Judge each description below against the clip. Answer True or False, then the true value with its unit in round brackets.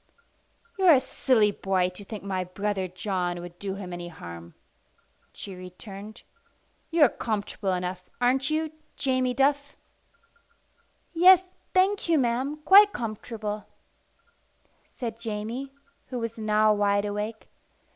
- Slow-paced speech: True (120 wpm)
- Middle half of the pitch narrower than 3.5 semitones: False (5.4 semitones)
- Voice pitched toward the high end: True (215 Hz)